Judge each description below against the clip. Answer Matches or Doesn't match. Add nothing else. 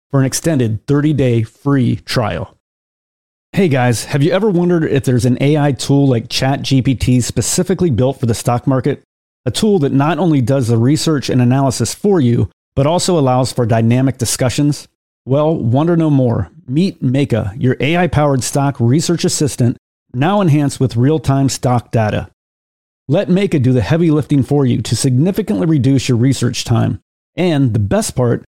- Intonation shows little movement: Doesn't match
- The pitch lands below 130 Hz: Doesn't match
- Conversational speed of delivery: Matches